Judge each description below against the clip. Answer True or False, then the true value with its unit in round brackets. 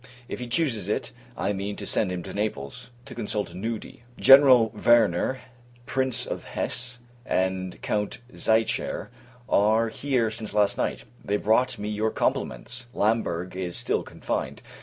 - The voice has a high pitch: False (110 Hz)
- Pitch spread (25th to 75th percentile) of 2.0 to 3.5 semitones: True (3.1 semitones)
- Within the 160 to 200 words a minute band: False (150 wpm)